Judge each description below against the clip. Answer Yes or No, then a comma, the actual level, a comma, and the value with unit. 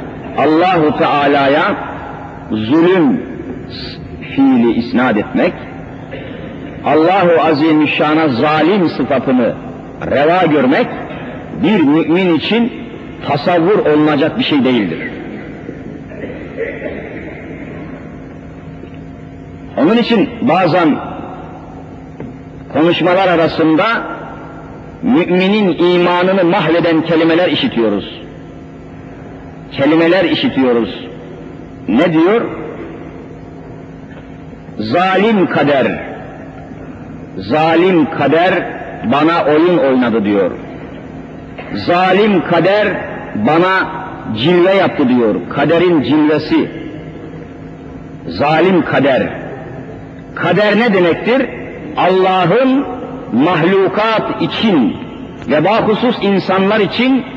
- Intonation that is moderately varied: Yes, average, 4.8 semitones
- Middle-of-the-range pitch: Yes, medium, 175 Hz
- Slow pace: Yes, slow, 65 wpm